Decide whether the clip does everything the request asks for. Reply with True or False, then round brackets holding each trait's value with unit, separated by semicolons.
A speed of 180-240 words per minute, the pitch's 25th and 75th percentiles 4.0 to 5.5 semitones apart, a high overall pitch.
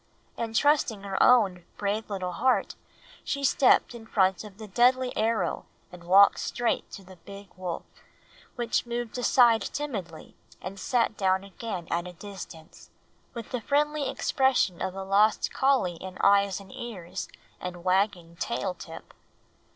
False (150 wpm; 4.4 semitones; 200 Hz)